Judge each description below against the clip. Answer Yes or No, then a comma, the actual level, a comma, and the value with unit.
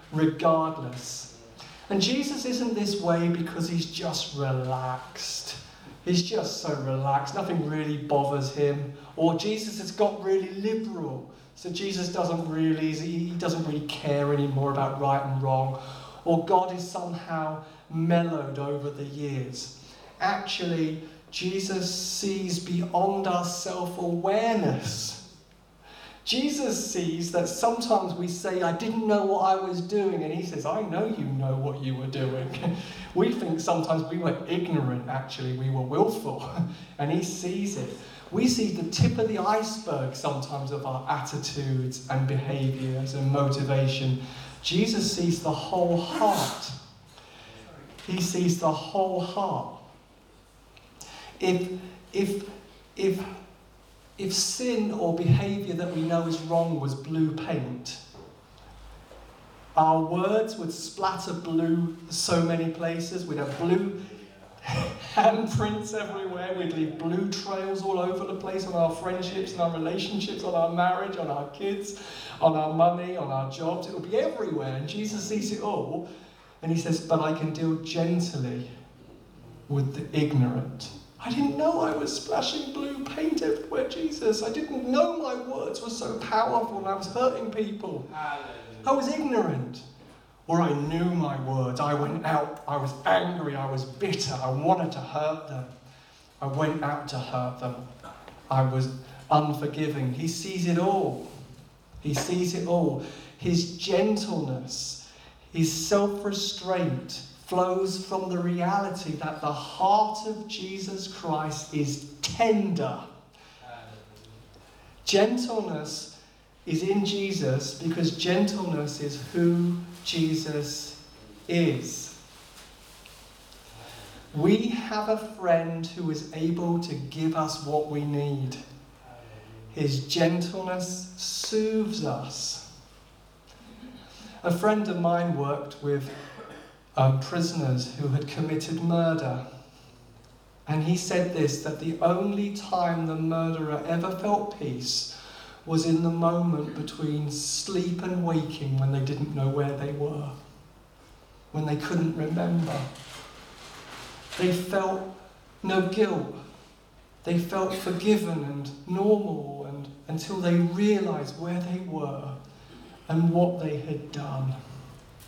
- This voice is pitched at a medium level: Yes, medium, 165 Hz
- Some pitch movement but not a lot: Yes, average, 4.8 semitones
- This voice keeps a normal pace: No, slow, 130 wpm